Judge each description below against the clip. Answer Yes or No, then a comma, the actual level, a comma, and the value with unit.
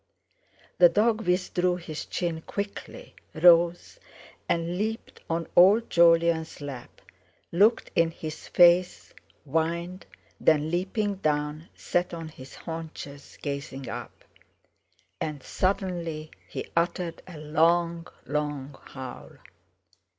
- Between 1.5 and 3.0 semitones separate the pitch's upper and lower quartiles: Yes, narrow, 2.6 semitones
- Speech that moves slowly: Yes, slow, 105 wpm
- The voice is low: No, medium, 170 Hz